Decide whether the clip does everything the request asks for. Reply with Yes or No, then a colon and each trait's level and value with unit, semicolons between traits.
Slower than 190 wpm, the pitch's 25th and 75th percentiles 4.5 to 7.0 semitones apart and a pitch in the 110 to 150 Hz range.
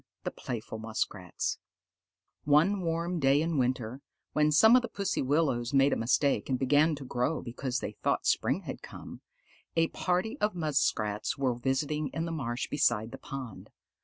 Yes: average, 165 wpm; average, 4.9 semitones; medium, 140 Hz